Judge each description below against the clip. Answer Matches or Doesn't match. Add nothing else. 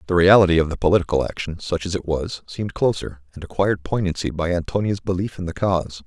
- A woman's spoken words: Doesn't match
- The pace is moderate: Doesn't match